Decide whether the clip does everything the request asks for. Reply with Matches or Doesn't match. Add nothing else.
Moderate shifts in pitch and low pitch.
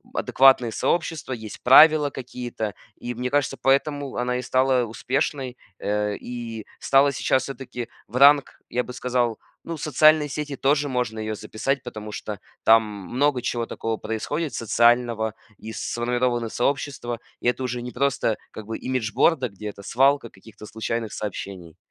Matches